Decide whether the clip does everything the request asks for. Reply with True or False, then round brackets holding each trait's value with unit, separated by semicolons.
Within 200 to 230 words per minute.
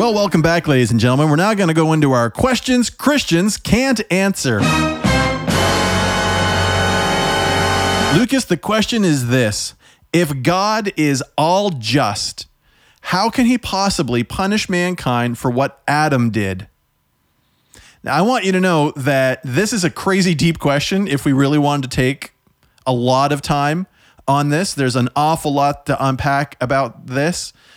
False (150 wpm)